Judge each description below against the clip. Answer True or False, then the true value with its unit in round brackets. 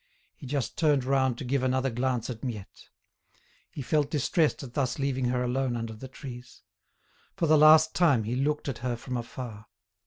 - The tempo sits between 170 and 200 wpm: True (185 wpm)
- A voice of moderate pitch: False (130 Hz)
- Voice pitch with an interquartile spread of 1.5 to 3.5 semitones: True (2.4 semitones)